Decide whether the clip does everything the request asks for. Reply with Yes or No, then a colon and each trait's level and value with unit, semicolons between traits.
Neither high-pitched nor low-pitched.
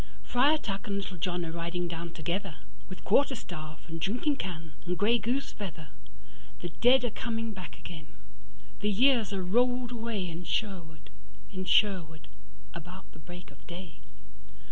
Yes: medium, 180 Hz